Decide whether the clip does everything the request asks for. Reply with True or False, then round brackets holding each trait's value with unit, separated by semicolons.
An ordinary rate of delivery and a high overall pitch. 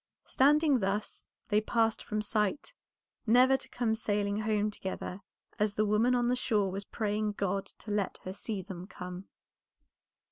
True (155 wpm; 210 Hz)